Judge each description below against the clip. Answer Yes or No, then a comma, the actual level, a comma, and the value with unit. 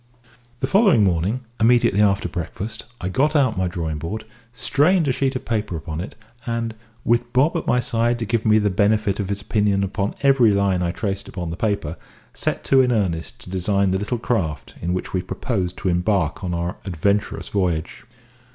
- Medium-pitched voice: No, low, 100 Hz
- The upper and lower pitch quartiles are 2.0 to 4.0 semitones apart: No, average, 4.5 semitones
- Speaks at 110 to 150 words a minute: No, average, 195 wpm